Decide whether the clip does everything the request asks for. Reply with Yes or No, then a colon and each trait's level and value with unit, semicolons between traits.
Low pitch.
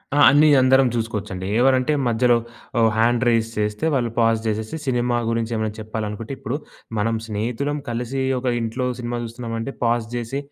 Yes: low, 115 Hz